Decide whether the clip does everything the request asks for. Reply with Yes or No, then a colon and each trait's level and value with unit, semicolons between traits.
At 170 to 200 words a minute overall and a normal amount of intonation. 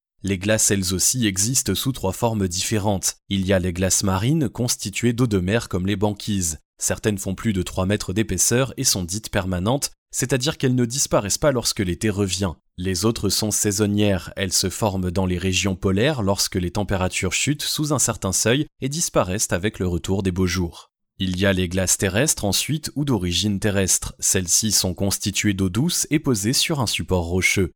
Yes: average, 190 wpm; average, 3.7 semitones